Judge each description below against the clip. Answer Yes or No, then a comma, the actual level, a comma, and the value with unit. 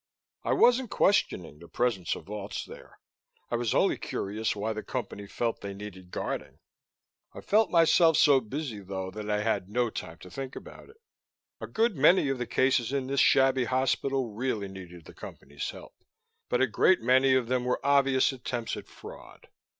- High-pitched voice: No, low, 120 Hz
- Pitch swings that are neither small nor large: Yes, average, 4.9 semitones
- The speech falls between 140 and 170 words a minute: No, average, 180 wpm